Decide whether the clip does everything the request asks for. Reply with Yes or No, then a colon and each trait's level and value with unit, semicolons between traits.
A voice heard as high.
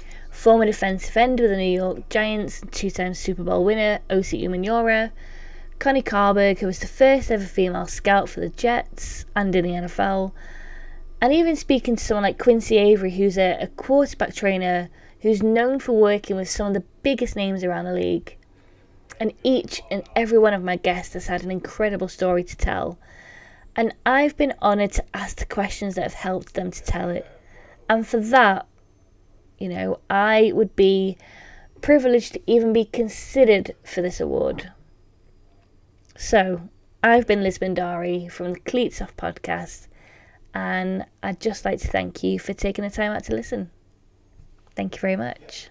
Yes: high, 195 Hz